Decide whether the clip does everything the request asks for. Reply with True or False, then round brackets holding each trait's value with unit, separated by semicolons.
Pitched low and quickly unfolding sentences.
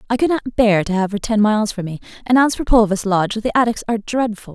False (220 Hz; 265 wpm)